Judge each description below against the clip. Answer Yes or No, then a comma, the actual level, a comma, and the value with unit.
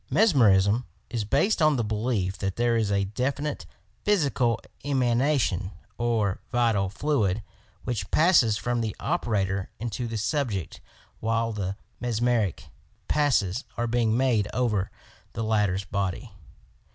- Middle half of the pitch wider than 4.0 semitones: No, average, 3.7 semitones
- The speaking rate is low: Yes, slow, 125 wpm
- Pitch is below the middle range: Yes, low, 115 Hz